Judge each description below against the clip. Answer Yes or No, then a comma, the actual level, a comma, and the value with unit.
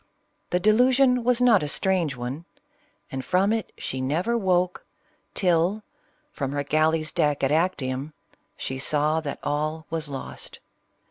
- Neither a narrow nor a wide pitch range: Yes, average, 4.9 semitones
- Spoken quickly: No, average, 140 wpm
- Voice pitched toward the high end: No, medium, 160 Hz